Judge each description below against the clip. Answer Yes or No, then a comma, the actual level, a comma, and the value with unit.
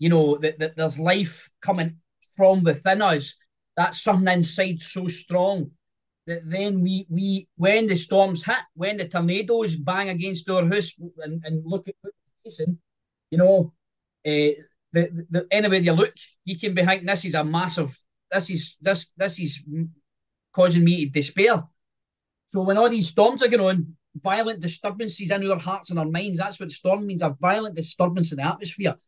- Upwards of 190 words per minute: No, average, 175 wpm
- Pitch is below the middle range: No, medium, 180 Hz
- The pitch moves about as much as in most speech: Yes, average, 3.1 semitones